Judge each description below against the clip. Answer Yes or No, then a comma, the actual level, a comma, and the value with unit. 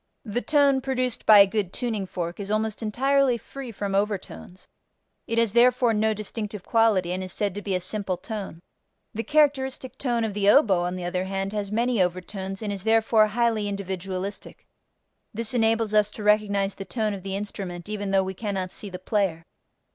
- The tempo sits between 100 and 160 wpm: No, average, 190 wpm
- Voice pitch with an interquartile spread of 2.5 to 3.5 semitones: Yes, average, 2.9 semitones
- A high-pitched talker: Yes, high, 210 Hz